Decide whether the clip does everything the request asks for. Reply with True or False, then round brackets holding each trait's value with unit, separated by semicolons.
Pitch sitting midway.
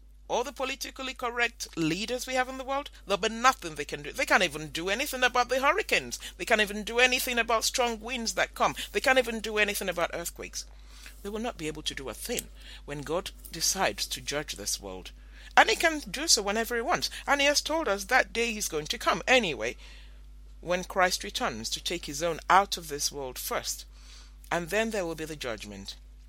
False (200 Hz)